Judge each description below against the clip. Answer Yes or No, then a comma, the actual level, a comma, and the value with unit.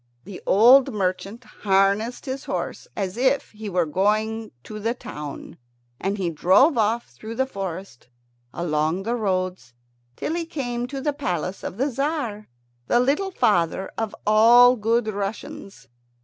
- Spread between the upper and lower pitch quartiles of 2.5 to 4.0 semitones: No, average, 4.5 semitones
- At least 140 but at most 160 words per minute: Yes, average, 150 wpm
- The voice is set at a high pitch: Yes, high, 215 Hz